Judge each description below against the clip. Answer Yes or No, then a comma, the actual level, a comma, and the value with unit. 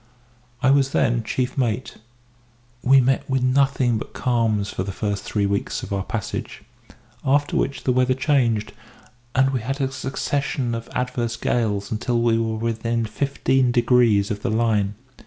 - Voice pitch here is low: Yes, low, 120 Hz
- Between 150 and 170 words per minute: Yes, average, 160 wpm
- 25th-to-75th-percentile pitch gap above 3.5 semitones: No, average, 3.1 semitones